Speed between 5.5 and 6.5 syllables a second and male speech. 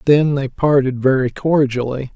No: 4.5 syllables/s; male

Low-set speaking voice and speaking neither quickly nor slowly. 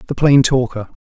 Yes: low, 130 Hz; average, 175 wpm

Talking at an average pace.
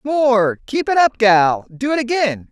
Yes: average, 190 wpm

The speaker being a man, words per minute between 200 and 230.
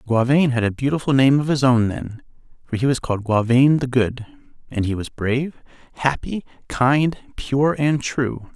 No: male; average, 175 wpm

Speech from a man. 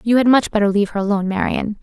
No: female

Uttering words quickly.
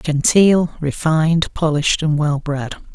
No: slow, 120 wpm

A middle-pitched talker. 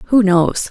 No: high, 200 Hz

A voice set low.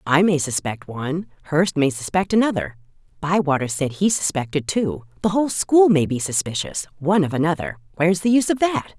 No: medium, 165 Hz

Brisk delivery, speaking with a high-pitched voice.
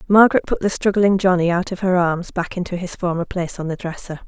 No: fast, 240 wpm; medium, 180 Hz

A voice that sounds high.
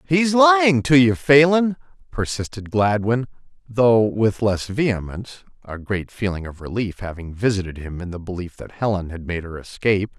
No: low, 110 Hz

